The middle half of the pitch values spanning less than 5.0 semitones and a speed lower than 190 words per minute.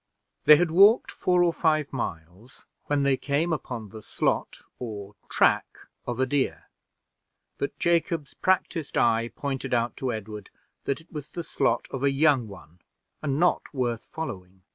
No: wide, 5.5 semitones; average, 160 wpm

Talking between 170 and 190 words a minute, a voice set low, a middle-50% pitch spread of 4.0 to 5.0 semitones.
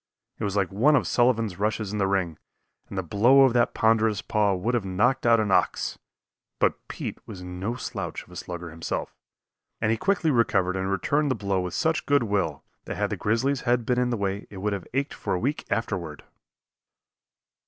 No: fast, 205 wpm; low, 105 Hz; average, 4.3 semitones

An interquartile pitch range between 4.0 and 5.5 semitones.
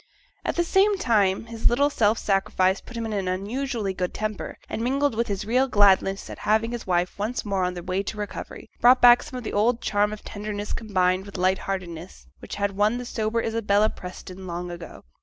No: average, 3.6 semitones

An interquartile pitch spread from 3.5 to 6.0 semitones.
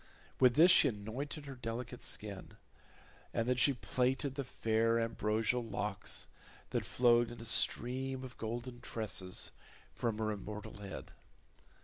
No: average, 2.8 semitones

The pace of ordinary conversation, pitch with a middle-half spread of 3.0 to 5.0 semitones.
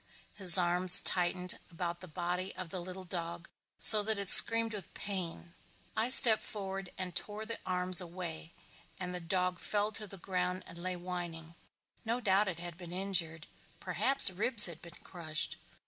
No: average, 170 wpm; narrow, 2.4 semitones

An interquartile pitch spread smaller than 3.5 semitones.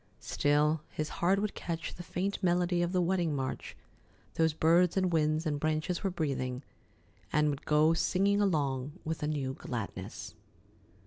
Yes: average, 3.1 semitones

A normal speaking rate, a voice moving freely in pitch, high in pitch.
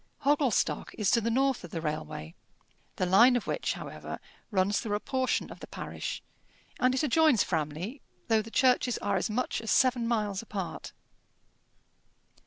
No: average, 165 wpm; average, 4.9 semitones; high, 225 Hz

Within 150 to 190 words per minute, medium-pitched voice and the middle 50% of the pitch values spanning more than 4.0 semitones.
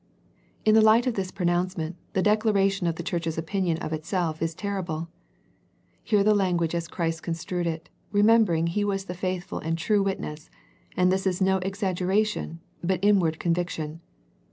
No: average, 175 wpm; medium, 180 Hz; average, 3.1 semitones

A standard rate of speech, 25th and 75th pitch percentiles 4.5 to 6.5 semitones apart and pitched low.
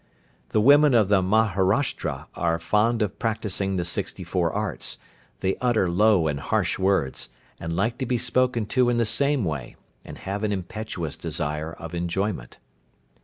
Yes: average, 165 wpm; average, 5.0 semitones; low, 100 Hz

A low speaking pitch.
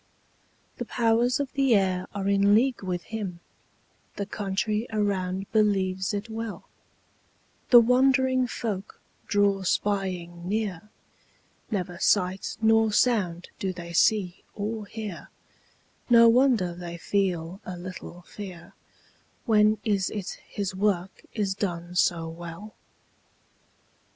No: high, 200 Hz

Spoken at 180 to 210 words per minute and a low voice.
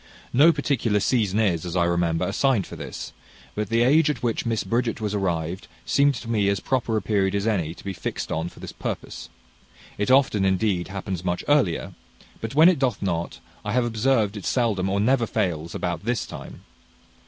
Yes: average, 200 wpm; low, 105 Hz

